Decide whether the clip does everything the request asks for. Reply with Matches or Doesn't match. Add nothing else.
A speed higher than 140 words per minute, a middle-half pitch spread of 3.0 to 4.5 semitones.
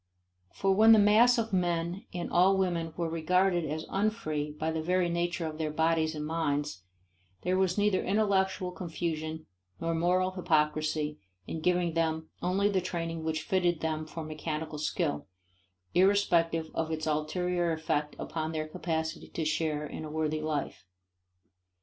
Doesn't match